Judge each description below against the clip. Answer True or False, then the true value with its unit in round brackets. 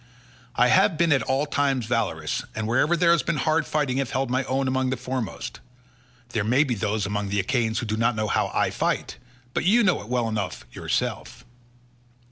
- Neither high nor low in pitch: False (125 Hz)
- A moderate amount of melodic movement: True (4.5 semitones)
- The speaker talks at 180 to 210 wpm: True (205 wpm)